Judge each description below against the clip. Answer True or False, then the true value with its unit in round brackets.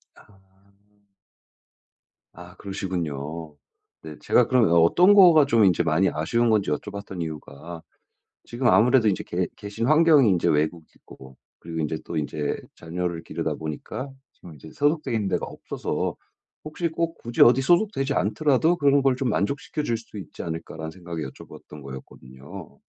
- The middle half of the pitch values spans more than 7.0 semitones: True (8.6 semitones)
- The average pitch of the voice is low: True (95 Hz)